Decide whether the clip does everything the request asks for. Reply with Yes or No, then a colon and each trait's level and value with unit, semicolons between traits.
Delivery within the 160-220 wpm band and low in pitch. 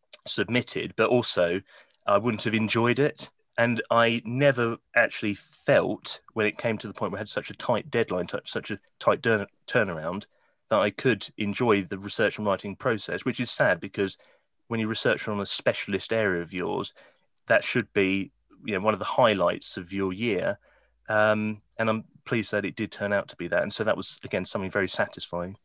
Yes: average, 200 wpm; low, 105 Hz